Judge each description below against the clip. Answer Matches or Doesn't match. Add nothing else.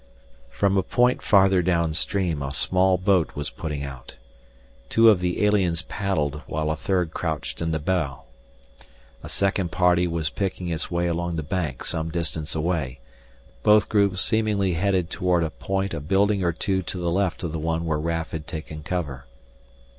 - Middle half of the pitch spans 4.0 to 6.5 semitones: Doesn't match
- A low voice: Matches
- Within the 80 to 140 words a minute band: Doesn't match